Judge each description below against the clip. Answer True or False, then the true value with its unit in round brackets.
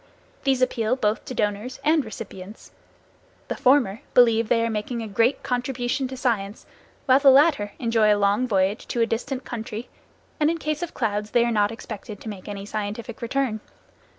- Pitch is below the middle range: False (230 Hz)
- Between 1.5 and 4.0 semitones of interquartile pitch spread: True (3.4 semitones)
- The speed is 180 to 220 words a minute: True (185 wpm)